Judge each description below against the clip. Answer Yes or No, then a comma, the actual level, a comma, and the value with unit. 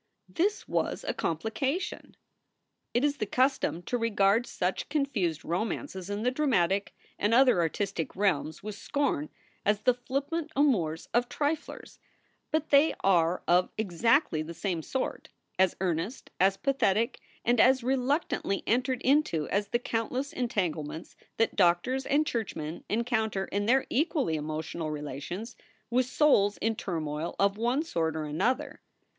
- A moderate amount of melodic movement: No, wide, 7.0 semitones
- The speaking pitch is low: No, high, 215 Hz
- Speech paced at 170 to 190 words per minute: No, average, 140 wpm